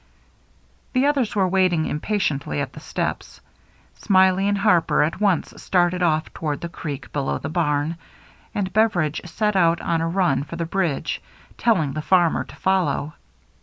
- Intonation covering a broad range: No, average, 3.7 semitones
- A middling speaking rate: Yes, average, 165 wpm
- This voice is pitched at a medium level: Yes, medium, 175 Hz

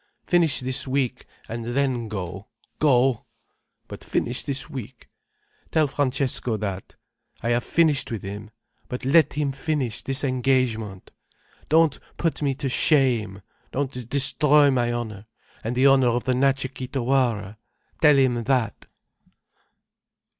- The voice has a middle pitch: No, low, 130 Hz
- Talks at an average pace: No, slow, 130 wpm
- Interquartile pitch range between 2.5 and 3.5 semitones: Yes, average, 3.0 semitones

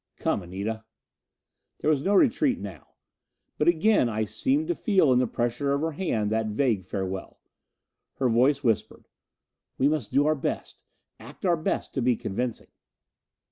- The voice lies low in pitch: Yes, low, 130 Hz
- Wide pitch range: Yes, wide, 6.1 semitones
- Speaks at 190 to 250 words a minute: No, average, 160 wpm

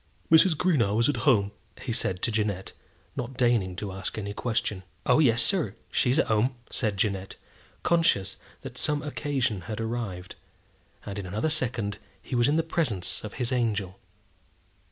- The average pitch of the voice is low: Yes, low, 115 Hz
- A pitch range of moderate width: Yes, average, 4.9 semitones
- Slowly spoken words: No, average, 170 wpm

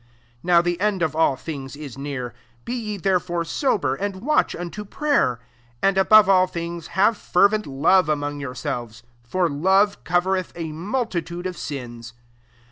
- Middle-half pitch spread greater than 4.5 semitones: Yes, average, 5.2 semitones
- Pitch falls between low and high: Yes, medium, 175 Hz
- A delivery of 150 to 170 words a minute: Yes, average, 160 wpm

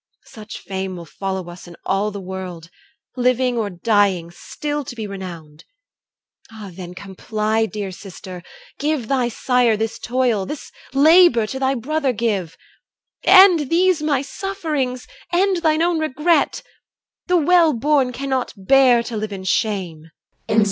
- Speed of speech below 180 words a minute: Yes, average, 140 wpm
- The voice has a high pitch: Yes, high, 235 Hz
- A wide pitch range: Yes, wide, 7.2 semitones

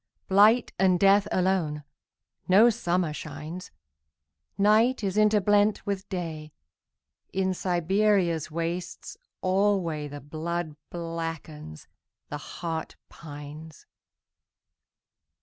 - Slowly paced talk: Yes, slow, 70 wpm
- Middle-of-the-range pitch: Yes, medium, 175 Hz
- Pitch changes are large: No, average, 4.3 semitones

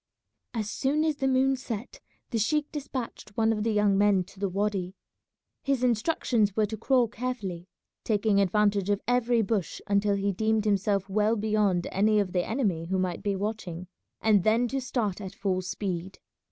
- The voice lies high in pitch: Yes, high, 210 Hz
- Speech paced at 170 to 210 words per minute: Yes, average, 180 wpm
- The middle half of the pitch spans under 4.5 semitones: Yes, average, 2.8 semitones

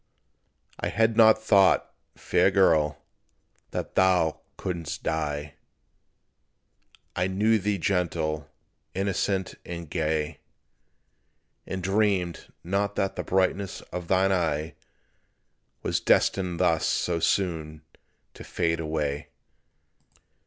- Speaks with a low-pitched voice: Yes, very low, 90 Hz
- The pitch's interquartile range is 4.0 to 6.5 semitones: No, average, 3.4 semitones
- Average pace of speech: No, slow, 100 wpm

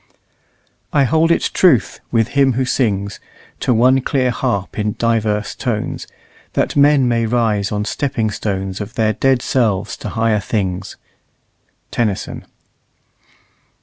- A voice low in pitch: Yes, low, 115 Hz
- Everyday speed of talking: No, slow, 130 wpm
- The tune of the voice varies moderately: Yes, average, 3.7 semitones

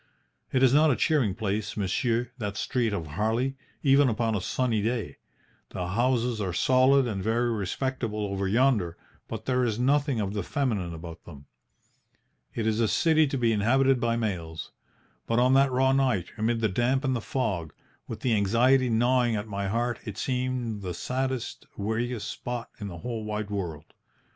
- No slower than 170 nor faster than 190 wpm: Yes, average, 175 wpm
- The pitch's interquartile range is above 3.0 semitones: Yes, average, 3.9 semitones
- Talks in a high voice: No, low, 115 Hz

